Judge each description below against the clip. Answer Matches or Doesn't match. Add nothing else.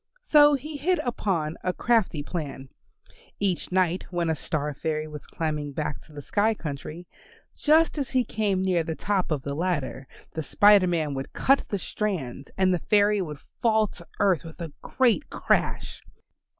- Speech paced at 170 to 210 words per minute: Matches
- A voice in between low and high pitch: Matches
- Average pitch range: Doesn't match